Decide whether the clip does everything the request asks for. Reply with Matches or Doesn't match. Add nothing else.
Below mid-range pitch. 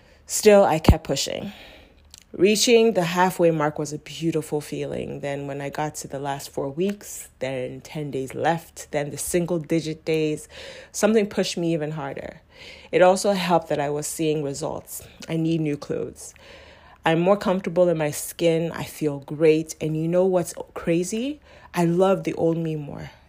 Doesn't match